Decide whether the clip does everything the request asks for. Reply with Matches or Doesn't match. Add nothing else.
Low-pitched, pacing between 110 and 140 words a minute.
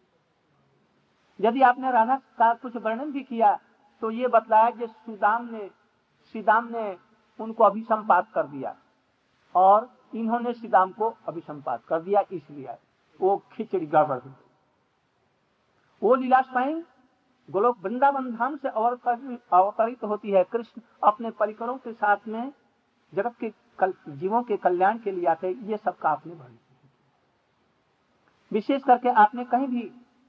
Doesn't match